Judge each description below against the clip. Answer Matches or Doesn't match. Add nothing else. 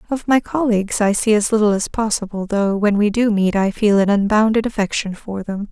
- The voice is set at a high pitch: Matches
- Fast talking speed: Matches